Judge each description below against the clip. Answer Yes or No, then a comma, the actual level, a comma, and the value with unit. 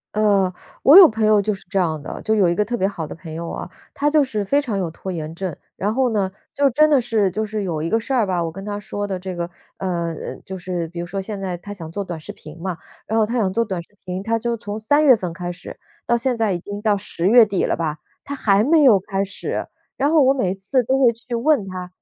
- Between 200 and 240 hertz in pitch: Yes, high, 205 Hz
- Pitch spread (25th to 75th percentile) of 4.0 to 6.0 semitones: Yes, average, 4.4 semitones